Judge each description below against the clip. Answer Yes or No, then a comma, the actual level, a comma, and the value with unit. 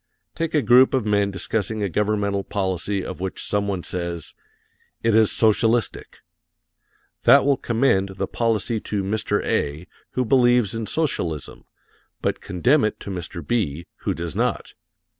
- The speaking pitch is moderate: No, low, 105 Hz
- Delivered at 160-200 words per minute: No, average, 150 wpm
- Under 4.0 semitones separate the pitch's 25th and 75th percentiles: Yes, average, 3.6 semitones